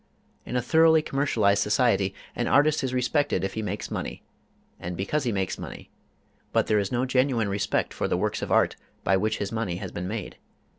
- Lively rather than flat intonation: No, average, 4.7 semitones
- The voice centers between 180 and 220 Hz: No, low, 110 Hz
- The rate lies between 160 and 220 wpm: Yes, average, 200 wpm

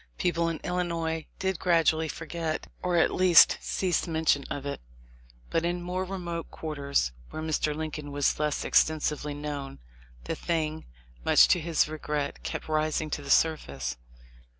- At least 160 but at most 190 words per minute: No, average, 150 wpm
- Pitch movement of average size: No, narrow, 2.3 semitones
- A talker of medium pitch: Yes, medium, 155 Hz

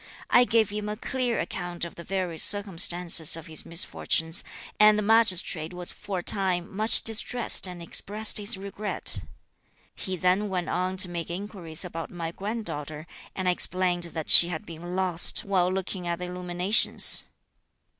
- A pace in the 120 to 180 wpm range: Yes, average, 165 wpm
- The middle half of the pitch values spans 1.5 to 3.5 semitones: Yes, average, 2.9 semitones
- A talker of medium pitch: Yes, medium, 180 Hz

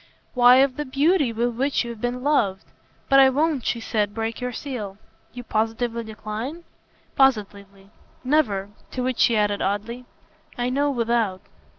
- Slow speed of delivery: No, average, 155 wpm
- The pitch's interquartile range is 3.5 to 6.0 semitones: Yes, average, 3.8 semitones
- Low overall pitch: No, high, 240 Hz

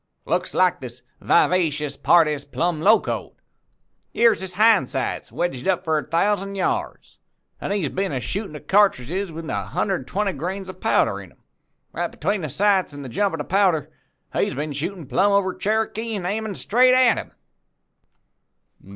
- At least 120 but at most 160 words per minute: No, average, 170 wpm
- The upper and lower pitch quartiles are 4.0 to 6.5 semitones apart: Yes, average, 5.0 semitones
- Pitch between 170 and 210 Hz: Yes, medium, 185 Hz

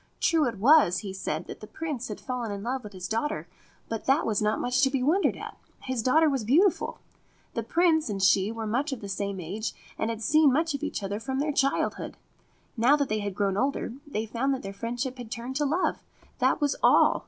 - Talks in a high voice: Yes, high, 245 Hz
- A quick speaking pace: Yes, fast, 235 wpm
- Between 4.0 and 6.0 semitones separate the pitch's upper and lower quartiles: Yes, average, 5.1 semitones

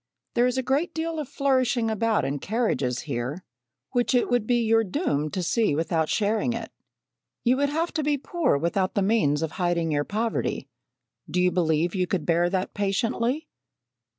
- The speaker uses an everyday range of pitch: No, wide, 6.5 semitones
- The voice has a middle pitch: No, high, 215 Hz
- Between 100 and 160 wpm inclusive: No, average, 180 wpm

